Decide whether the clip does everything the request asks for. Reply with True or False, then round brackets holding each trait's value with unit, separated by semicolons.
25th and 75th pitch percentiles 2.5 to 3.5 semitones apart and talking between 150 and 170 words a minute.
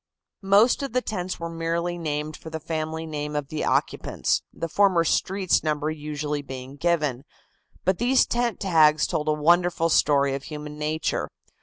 True (2.8 semitones; 165 wpm)